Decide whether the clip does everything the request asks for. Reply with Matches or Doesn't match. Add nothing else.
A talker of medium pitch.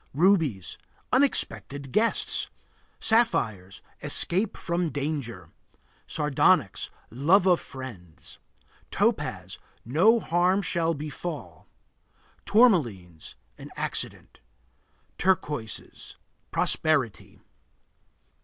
Matches